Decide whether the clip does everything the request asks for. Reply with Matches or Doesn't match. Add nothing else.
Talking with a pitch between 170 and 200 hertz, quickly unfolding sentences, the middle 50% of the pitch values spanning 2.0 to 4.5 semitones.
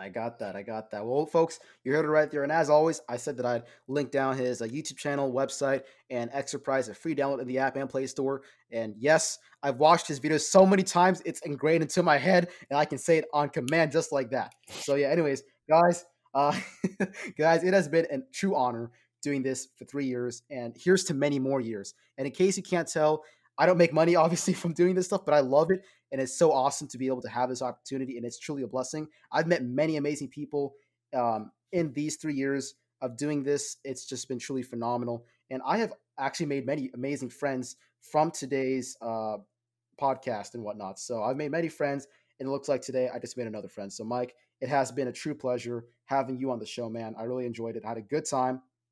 Doesn't match